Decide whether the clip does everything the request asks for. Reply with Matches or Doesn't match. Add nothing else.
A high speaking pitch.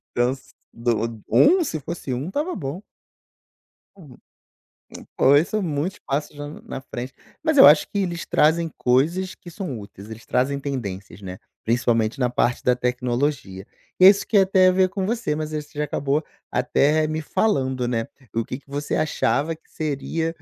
Doesn't match